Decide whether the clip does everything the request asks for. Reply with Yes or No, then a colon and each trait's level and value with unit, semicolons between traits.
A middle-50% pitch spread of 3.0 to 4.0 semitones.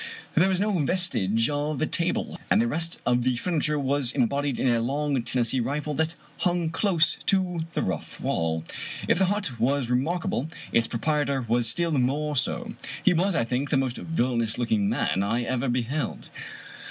No: average, 5.3 semitones